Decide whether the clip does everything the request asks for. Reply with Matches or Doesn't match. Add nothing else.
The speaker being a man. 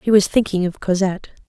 Doesn't match